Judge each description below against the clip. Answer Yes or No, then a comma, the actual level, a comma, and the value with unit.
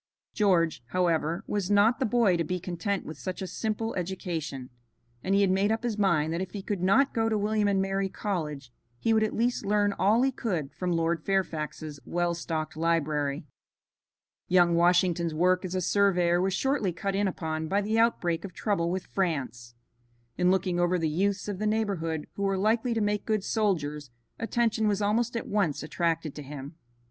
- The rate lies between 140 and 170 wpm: No, average, 195 wpm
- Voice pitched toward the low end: No, medium, 185 Hz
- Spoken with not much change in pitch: No, average, 3.8 semitones